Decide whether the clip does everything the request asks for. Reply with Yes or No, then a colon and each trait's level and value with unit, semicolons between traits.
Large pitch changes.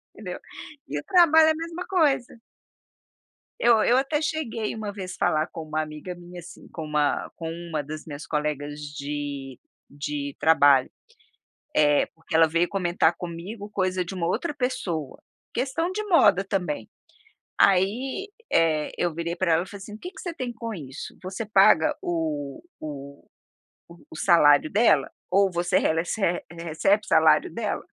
Yes: wide, 6.2 semitones